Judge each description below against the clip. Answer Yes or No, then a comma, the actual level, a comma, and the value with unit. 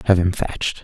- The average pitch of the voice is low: Yes, very low, 90 Hz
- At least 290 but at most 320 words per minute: No, fast, 215 wpm